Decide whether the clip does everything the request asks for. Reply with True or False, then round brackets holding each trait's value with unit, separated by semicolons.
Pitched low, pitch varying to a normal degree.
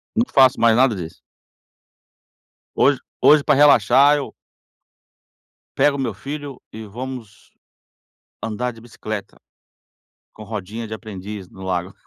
True (115 Hz; 4.3 semitones)